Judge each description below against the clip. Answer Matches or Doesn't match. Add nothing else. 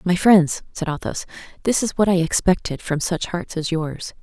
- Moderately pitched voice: Matches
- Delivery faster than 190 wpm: Matches